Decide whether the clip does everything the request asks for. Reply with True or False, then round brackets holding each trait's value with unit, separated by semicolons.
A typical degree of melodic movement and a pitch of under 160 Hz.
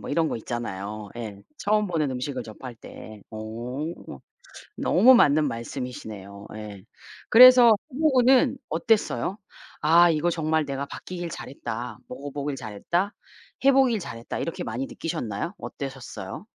False (7.1 semitones; 140 Hz)